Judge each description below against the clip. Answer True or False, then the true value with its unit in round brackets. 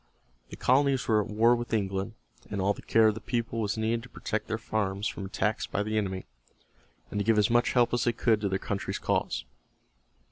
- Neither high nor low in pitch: False (110 Hz)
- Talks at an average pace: False (220 wpm)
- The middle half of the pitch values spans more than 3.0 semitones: False (2.5 semitones)